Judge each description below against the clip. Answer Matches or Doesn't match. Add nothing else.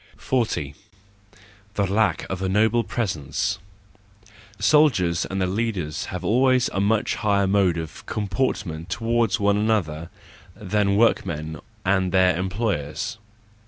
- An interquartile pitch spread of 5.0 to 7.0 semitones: Doesn't match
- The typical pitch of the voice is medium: Doesn't match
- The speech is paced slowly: Matches